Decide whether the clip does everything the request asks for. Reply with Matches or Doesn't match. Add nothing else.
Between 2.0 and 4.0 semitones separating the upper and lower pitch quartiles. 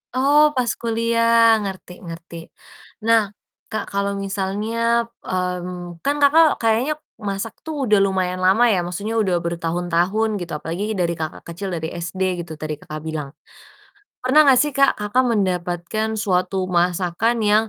Doesn't match